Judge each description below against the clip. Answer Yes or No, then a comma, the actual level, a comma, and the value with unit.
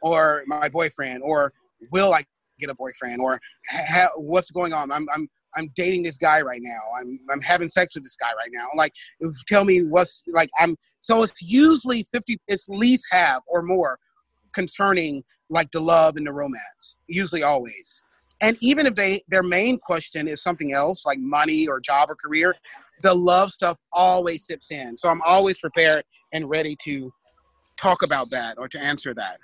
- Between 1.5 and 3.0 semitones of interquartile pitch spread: No, average, 4.1 semitones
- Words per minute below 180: No, average, 185 wpm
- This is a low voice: No, medium, 165 Hz